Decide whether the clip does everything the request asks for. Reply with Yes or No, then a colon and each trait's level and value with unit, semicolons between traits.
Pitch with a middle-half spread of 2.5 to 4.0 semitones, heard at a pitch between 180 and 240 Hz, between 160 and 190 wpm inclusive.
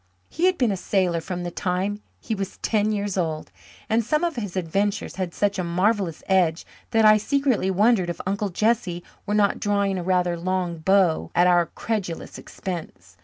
Yes: average, 3.2 semitones; high, 190 Hz; average, 185 wpm